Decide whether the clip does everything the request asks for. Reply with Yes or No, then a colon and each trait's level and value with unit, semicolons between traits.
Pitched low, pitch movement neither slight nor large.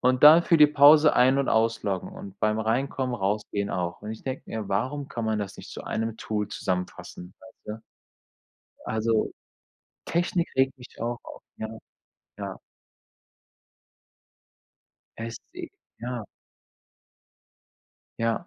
Yes: low, 115 Hz; average, 4.5 semitones